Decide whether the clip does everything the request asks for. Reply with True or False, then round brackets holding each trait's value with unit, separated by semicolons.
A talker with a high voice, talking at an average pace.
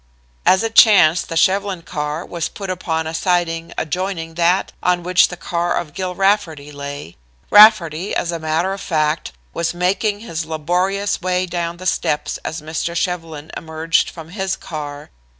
False (170 Hz; 165 wpm)